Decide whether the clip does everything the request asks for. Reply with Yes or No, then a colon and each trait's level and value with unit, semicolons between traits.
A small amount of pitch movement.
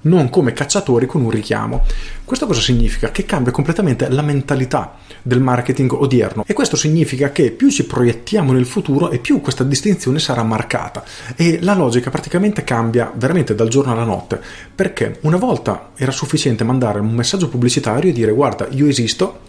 No: average, 4.3 semitones